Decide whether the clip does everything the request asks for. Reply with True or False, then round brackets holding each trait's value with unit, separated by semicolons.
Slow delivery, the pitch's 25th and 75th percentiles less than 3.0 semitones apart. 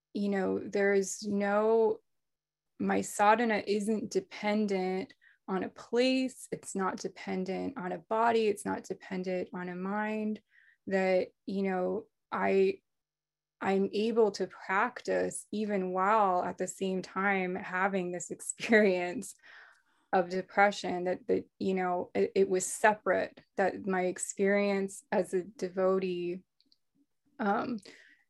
True (125 wpm; 2.6 semitones)